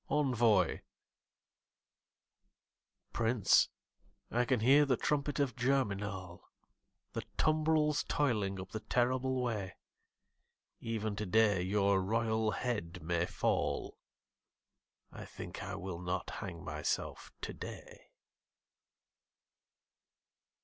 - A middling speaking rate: No, slow, 90 wpm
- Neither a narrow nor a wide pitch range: Yes, average, 4.9 semitones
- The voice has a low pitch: Yes, low, 110 Hz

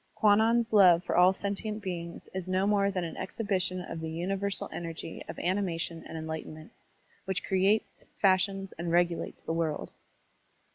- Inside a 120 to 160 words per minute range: Yes, average, 150 wpm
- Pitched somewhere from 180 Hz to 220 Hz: Yes, medium, 185 Hz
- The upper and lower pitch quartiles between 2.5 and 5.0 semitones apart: Yes, average, 2.9 semitones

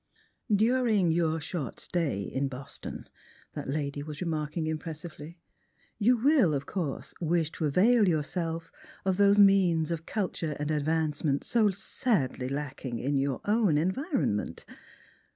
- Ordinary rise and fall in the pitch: Yes, average, 5.0 semitones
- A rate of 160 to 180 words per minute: No, slow, 135 wpm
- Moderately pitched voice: Yes, medium, 160 Hz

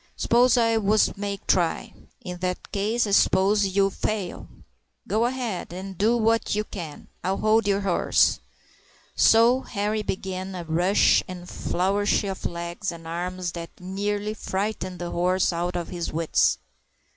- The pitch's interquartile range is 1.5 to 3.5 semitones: Yes, average, 3.1 semitones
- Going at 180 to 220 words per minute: No, average, 165 wpm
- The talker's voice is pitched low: No, high, 195 Hz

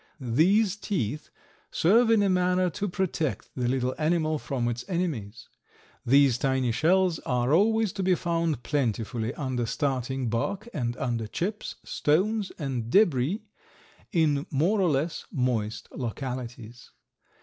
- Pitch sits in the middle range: Yes, medium, 145 Hz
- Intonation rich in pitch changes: Yes, wide, 6.8 semitones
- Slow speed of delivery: Yes, slow, 130 wpm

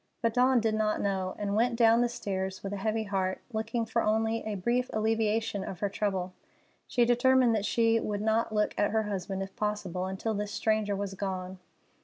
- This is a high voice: Yes, high, 215 Hz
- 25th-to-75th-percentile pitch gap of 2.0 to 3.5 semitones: Yes, narrow, 2.5 semitones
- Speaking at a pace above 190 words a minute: Yes, average, 200 wpm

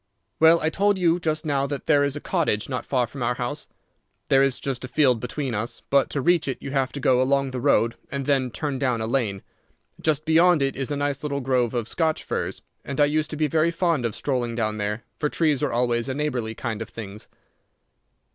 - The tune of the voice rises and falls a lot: No, average, 3.6 semitones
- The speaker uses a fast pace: Yes, fast, 230 wpm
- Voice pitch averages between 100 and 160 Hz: Yes, low, 135 Hz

